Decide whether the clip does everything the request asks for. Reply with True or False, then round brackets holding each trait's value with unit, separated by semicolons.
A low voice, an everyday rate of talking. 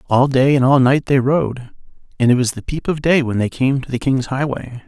False (130 Hz; 260 wpm)